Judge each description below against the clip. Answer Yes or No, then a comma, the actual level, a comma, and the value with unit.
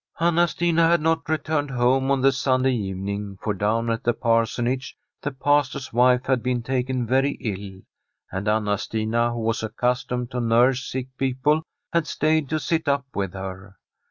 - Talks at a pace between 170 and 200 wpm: Yes, average, 180 wpm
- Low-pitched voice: Yes, low, 125 Hz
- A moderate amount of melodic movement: Yes, average, 3.7 semitones